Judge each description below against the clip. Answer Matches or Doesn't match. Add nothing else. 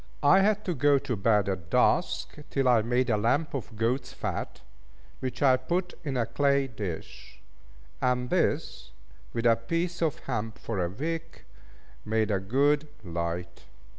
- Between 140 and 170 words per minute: Matches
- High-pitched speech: Doesn't match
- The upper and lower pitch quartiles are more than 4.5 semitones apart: Matches